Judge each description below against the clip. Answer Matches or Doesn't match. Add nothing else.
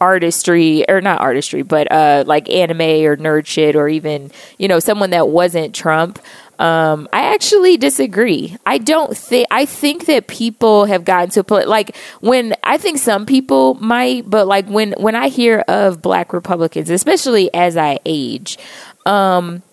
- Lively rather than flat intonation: Matches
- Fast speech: Doesn't match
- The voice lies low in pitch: Doesn't match